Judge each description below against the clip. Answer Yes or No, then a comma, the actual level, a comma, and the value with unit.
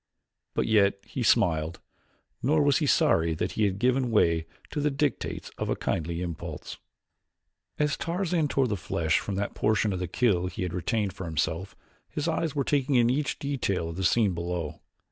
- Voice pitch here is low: Yes, low, 105 Hz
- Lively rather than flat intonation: Yes, wide, 8.1 semitones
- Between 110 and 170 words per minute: No, average, 185 wpm